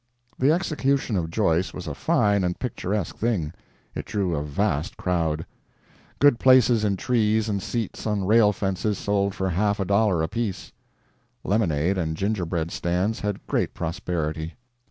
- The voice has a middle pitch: No, low, 100 Hz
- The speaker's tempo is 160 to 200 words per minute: No, average, 150 wpm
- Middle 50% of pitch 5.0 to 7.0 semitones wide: No, average, 4.0 semitones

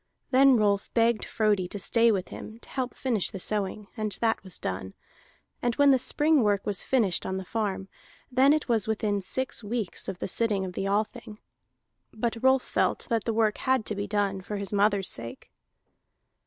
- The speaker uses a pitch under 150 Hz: No, high, 215 Hz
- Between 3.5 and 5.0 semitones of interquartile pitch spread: No, average, 3.0 semitones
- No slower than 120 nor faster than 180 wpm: No, average, 195 wpm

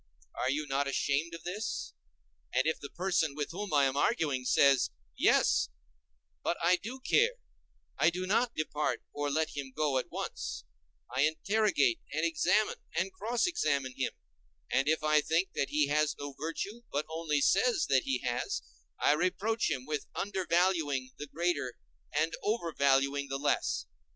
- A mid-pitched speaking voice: Yes, medium, 155 Hz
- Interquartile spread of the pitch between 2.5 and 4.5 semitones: No, average, 4.9 semitones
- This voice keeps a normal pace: Yes, average, 160 wpm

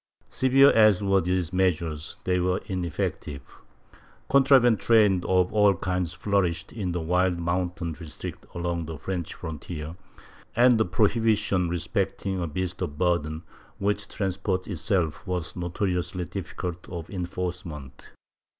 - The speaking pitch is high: No, very low, 90 Hz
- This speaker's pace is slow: Yes, slow, 130 wpm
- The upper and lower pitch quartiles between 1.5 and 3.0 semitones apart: Yes, narrow, 2.5 semitones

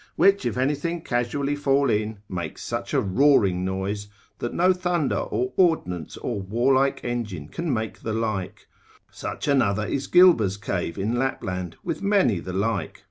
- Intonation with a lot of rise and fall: Yes, wide, 6.3 semitones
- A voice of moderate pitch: No, low, 120 Hz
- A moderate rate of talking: Yes, average, 155 wpm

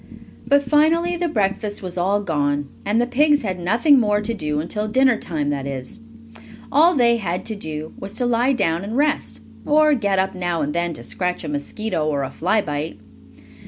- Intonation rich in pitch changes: Yes, wide, 7.3 semitones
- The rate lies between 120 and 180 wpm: No, average, 195 wpm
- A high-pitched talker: Yes, high, 205 Hz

